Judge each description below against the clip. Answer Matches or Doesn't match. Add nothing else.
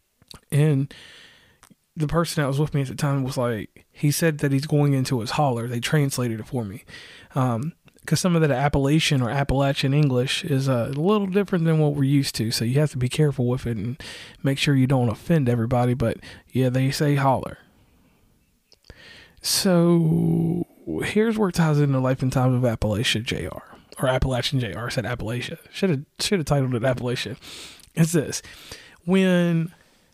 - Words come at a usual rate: Matches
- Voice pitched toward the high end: Doesn't match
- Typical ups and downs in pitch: Matches